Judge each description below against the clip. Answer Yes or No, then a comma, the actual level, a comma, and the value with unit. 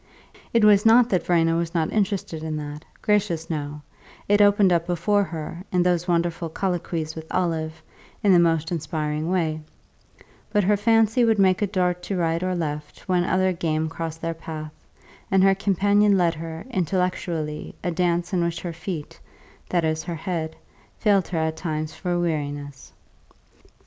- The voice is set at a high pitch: No, medium, 170 Hz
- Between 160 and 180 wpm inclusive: Yes, average, 170 wpm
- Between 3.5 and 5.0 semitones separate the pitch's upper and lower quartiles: No, average, 3.0 semitones